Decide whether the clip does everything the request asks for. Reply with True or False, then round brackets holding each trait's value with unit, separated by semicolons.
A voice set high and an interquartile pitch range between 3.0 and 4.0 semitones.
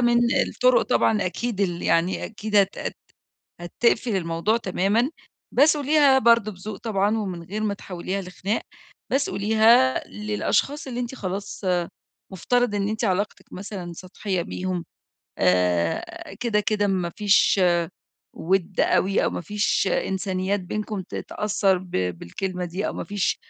True (200 Hz; 3.4 semitones)